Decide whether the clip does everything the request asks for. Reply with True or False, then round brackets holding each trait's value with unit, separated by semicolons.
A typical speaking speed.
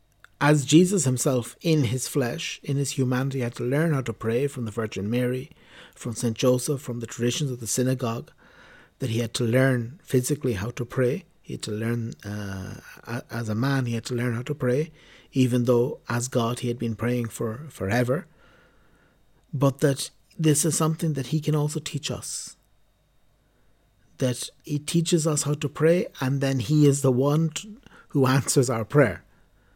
True (185 wpm)